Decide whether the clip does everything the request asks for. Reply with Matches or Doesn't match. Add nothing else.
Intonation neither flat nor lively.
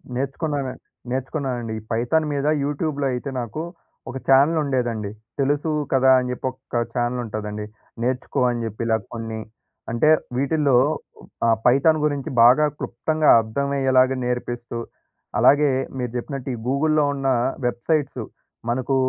Matches